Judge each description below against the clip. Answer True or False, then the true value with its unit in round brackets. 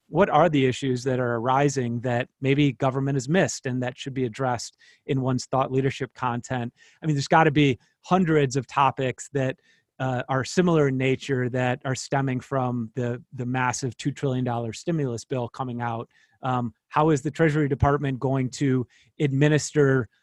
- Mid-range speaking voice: False (130 Hz)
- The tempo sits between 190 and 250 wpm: False (180 wpm)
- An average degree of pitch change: False (2.1 semitones)